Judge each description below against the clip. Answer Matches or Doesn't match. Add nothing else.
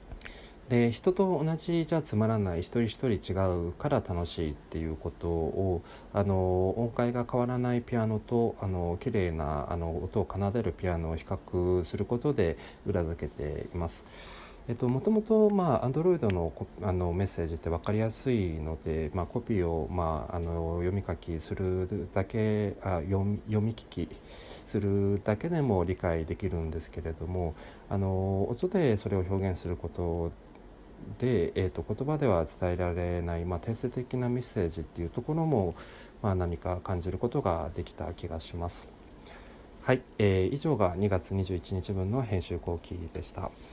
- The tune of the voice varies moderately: Matches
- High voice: Doesn't match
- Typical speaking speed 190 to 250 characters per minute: Doesn't match